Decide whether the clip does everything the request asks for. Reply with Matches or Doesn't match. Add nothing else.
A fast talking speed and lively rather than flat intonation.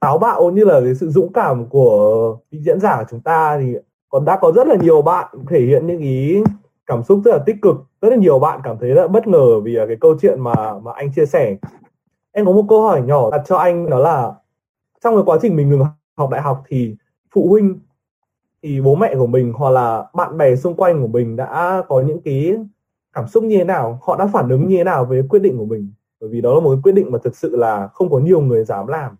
Matches